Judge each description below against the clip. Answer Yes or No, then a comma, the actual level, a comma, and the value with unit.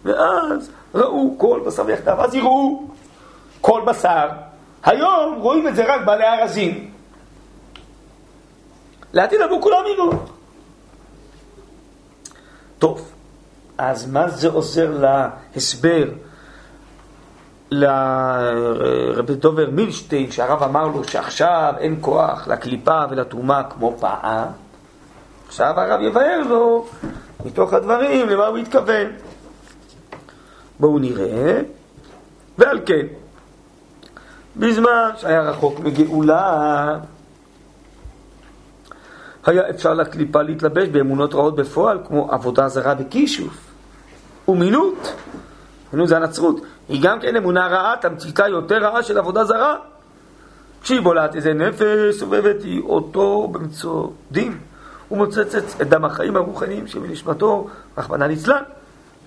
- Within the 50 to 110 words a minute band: Yes, slow, 100 wpm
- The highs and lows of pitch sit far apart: Yes, wide, 7.9 semitones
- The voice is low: No, medium, 165 Hz